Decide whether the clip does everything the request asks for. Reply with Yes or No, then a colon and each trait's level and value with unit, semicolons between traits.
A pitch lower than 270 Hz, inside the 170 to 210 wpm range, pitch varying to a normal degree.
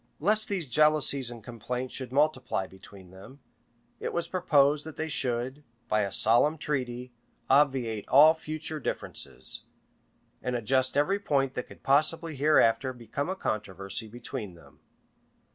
No: low, 135 Hz; average, 145 wpm; average, 4.3 semitones